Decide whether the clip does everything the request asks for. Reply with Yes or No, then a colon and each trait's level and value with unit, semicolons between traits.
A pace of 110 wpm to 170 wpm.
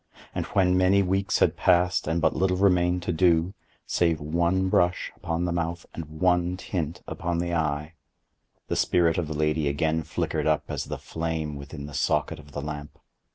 No: average, 185 wpm